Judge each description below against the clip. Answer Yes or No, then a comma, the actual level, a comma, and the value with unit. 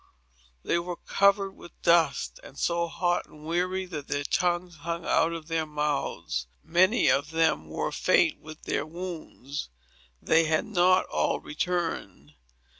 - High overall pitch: No, medium, 170 Hz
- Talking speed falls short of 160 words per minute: Yes, average, 140 wpm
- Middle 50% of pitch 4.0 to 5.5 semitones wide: No, average, 2.7 semitones